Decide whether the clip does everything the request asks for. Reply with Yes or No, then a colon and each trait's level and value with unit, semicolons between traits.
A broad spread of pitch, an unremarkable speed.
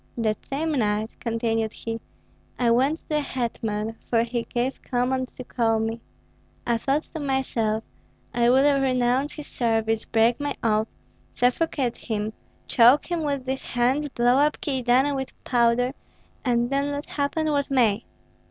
No: average, 3.3 semitones; average, 150 wpm